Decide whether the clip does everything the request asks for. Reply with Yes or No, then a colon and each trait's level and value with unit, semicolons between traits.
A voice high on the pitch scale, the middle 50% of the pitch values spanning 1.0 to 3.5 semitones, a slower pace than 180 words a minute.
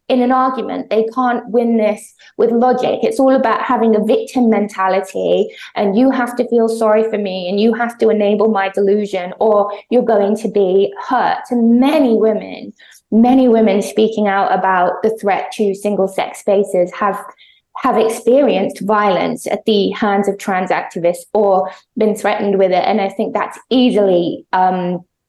Yes: high, 215 Hz; average, 3.1 semitones; average, 170 wpm